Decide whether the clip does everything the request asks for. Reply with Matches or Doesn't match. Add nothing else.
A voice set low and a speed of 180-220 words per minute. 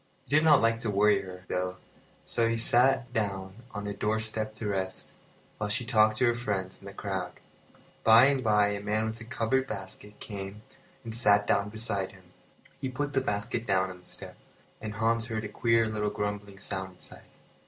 Matches